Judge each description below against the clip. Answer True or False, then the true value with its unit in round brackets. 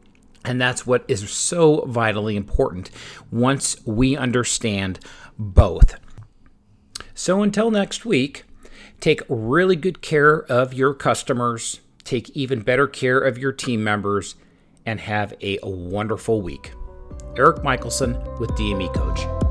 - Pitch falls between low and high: False (120 Hz)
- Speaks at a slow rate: True (125 wpm)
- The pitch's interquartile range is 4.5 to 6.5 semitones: True (5.1 semitones)